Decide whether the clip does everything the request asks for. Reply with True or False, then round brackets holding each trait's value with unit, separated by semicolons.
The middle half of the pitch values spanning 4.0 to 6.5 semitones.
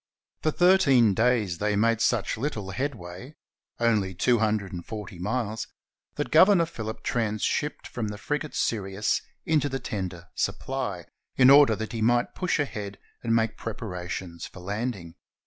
True (4.6 semitones)